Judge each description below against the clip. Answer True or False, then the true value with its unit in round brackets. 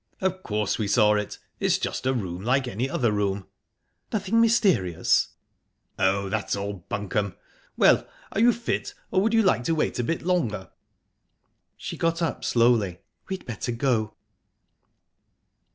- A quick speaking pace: False (145 wpm)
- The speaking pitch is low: True (120 Hz)